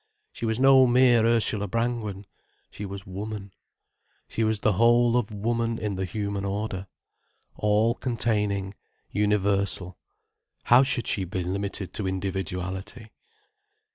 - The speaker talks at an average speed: No, slow, 125 wpm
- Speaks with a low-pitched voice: Yes, low, 105 Hz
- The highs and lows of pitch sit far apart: No, average, 3.0 semitones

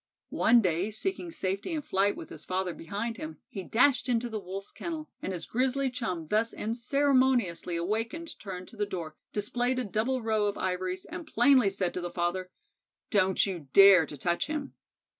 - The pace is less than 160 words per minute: No, average, 180 wpm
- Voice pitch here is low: No, high, 210 Hz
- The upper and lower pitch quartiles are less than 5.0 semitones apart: No, wide, 5.5 semitones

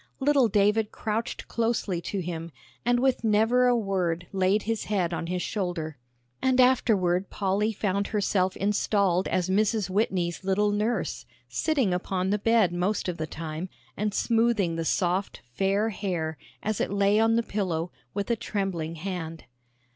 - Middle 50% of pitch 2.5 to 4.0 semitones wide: Yes, average, 3.4 semitones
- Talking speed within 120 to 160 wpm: Yes, average, 155 wpm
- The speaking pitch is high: Yes, high, 200 Hz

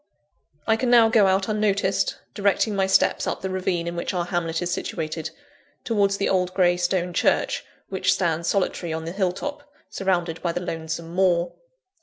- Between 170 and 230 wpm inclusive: Yes, average, 180 wpm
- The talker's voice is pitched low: No, medium, 185 Hz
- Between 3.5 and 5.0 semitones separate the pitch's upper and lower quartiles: No, narrow, 2.6 semitones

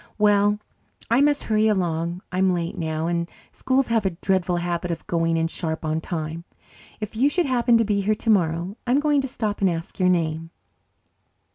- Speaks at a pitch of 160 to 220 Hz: Yes, medium, 185 Hz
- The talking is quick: No, average, 185 wpm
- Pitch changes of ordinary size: Yes, average, 4.7 semitones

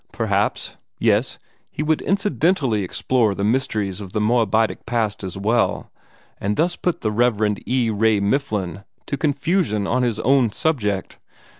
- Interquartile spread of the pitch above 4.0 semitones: Yes, average, 4.7 semitones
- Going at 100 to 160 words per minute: Yes, average, 145 wpm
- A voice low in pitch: Yes, low, 115 Hz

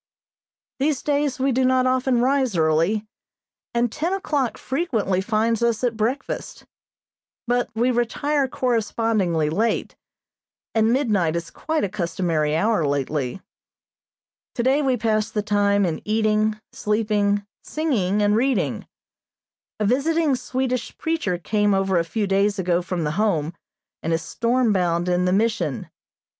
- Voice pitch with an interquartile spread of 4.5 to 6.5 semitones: Yes, average, 5.2 semitones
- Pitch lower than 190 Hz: No, high, 215 Hz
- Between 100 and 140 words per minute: Yes, slow, 135 wpm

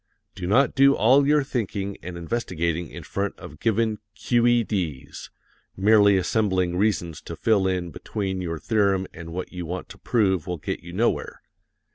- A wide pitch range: No, average, 4.1 semitones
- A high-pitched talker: No, very low, 95 Hz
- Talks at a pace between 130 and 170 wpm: Yes, average, 160 wpm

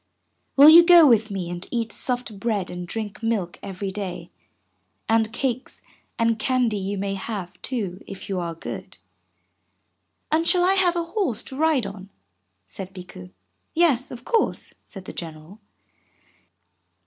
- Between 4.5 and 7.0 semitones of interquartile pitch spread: Yes, wide, 5.6 semitones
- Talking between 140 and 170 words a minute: Yes, average, 150 wpm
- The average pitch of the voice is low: No, high, 220 Hz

